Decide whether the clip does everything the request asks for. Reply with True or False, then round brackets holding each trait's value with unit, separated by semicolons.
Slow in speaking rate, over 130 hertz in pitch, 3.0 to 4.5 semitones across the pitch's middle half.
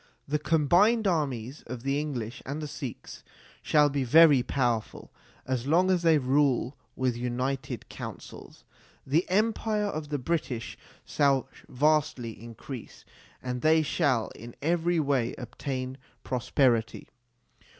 True (130 wpm; 140 Hz; 3.9 semitones)